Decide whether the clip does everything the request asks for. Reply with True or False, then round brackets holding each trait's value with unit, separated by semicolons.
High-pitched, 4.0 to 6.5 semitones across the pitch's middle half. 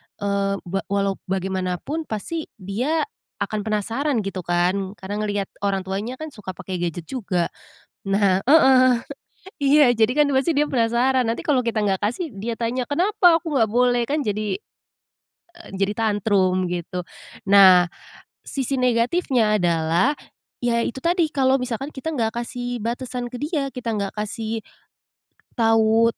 True (225 Hz; 5.0 semitones)